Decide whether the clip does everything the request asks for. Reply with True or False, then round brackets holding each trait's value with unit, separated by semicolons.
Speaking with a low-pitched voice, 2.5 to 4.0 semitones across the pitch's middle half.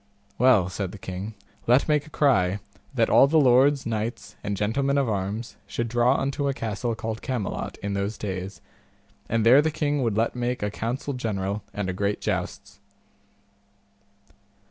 False (115 Hz; 4.4 semitones)